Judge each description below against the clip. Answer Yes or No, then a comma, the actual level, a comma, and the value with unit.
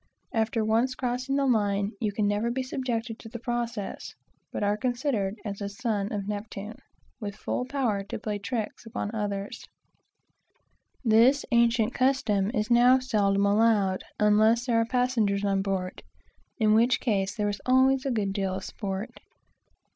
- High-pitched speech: Yes, high, 220 Hz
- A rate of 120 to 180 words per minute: Yes, average, 160 wpm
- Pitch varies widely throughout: No, average, 3.1 semitones